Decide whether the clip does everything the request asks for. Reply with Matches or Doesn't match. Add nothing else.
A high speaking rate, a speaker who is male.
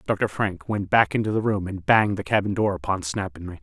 Matches